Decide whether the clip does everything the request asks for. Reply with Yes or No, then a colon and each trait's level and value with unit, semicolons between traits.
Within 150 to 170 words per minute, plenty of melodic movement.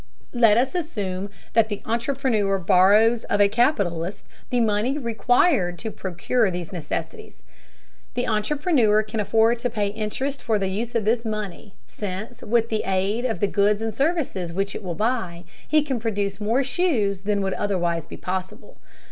No: average, 165 wpm; average, 3.5 semitones